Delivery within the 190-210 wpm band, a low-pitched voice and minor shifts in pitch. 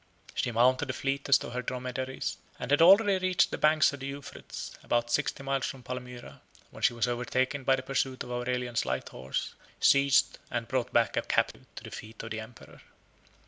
Yes: average, 200 wpm; low, 130 Hz; narrow, 2.2 semitones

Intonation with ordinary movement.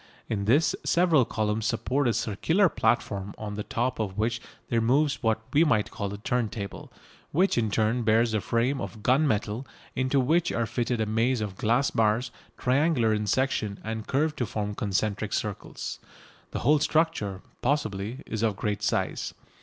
Yes: average, 3.7 semitones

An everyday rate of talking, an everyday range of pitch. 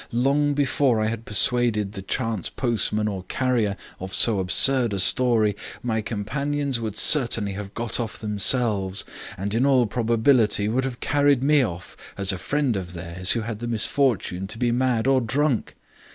Yes: average, 170 wpm; average, 3.9 semitones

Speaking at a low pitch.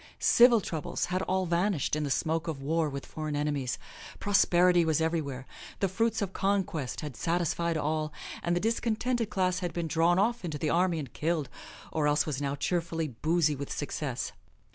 No: medium, 165 Hz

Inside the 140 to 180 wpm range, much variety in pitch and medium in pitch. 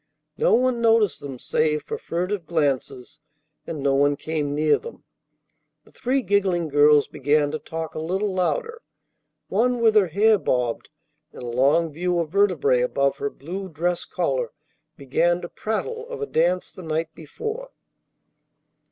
Yes: average, 155 wpm; wide, 6.1 semitones; medium, 170 Hz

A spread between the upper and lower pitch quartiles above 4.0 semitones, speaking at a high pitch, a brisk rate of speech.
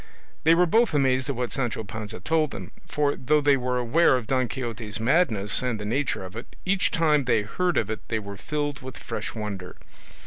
No: average, 5.2 semitones; low, 125 Hz; fast, 210 wpm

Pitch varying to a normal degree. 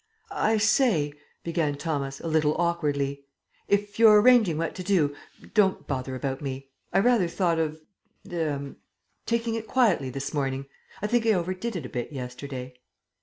No: wide, 6.6 semitones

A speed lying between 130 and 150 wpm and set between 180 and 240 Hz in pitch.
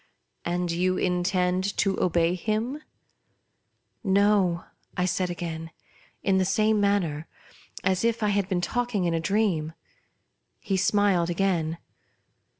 Yes: average, 140 wpm; medium, 185 Hz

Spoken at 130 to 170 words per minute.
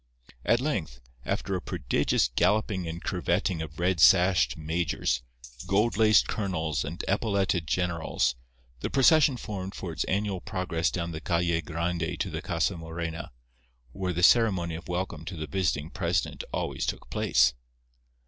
Yes: average, 150 wpm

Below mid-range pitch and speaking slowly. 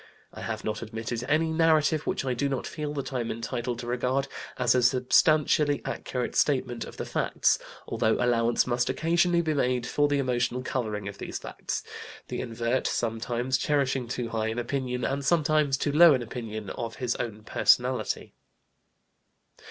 No: low, 125 Hz; average, 170 wpm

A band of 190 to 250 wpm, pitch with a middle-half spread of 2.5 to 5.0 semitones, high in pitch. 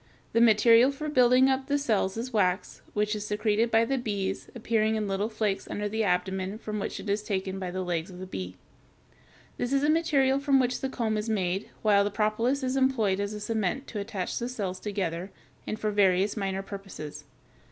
Yes: fast, 205 wpm; average, 3.6 semitones; high, 210 Hz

